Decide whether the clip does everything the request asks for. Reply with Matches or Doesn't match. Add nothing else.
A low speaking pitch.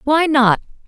Doesn't match